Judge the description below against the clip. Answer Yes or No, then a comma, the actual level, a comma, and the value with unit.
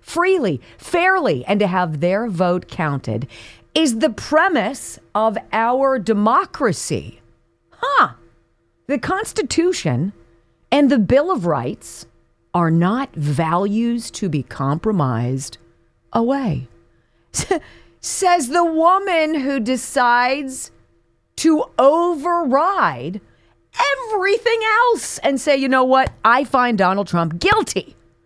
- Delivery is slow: Yes, slow, 100 wpm